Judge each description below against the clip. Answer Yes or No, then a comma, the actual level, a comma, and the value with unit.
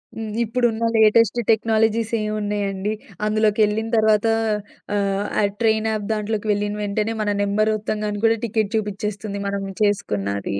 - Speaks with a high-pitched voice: Yes, high, 215 Hz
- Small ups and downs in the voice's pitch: Yes, narrow, 1.3 semitones